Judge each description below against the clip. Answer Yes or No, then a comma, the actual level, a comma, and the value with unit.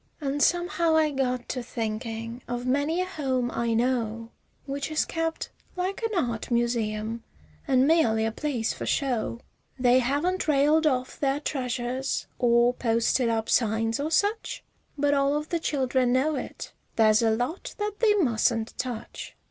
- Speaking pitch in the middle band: No, very high, 255 Hz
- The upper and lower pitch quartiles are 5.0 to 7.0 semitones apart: No, average, 4.5 semitones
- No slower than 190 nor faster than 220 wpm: No, average, 155 wpm